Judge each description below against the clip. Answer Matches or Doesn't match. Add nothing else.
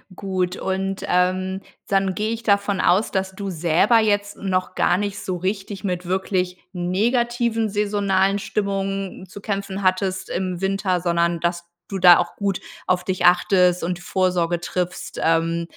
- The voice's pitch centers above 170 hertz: Matches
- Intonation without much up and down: Matches